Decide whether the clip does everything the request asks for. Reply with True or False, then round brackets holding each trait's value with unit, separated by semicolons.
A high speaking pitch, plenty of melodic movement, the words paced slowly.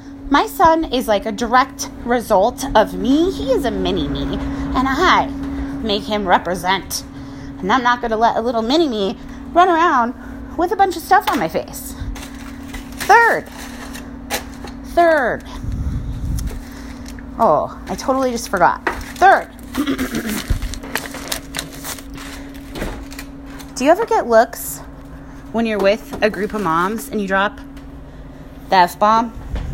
False (255 Hz; 4.9 semitones; 130 wpm)